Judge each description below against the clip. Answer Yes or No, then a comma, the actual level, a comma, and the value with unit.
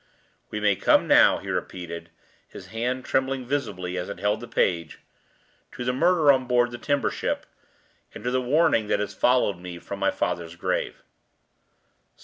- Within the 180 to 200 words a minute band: No, average, 170 wpm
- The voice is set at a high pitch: No, low, 115 Hz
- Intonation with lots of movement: Yes, wide, 5.8 semitones